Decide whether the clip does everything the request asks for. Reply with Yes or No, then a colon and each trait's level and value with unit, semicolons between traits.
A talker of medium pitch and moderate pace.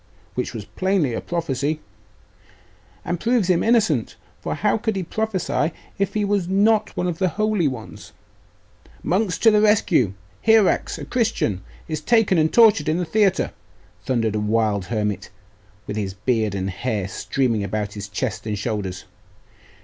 Yes: medium, 155 Hz; average, 155 wpm